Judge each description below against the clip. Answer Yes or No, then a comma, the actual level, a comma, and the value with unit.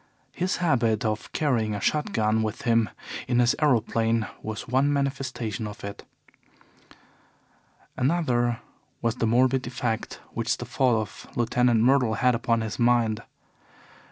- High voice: No, low, 120 Hz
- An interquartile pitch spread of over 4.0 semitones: No, average, 2.7 semitones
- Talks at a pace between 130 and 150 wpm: Yes, slow, 135 wpm